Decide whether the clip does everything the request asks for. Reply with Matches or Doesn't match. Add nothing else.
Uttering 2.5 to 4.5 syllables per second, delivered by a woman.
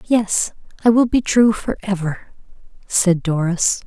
Matches